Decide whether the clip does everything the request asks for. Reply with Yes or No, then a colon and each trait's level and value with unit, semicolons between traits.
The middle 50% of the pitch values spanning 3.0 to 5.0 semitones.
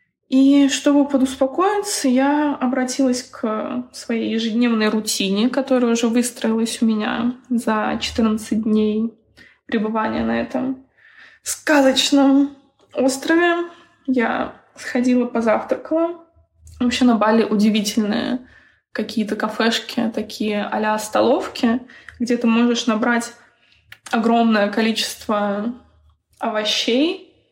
Yes: average, 3.5 semitones